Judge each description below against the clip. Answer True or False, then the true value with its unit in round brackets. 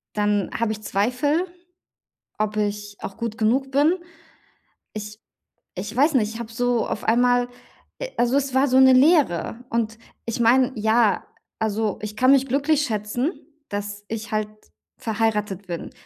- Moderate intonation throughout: True (3.6 semitones)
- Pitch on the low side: False (225 Hz)